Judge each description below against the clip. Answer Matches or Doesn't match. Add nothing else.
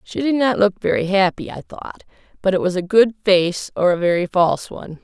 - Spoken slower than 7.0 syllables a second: Matches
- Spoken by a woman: Matches